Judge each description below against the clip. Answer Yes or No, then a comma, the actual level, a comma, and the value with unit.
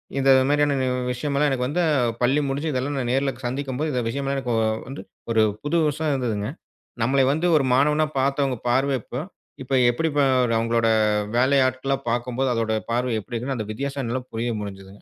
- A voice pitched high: No, low, 130 Hz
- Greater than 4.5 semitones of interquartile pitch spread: No, average, 2.7 semitones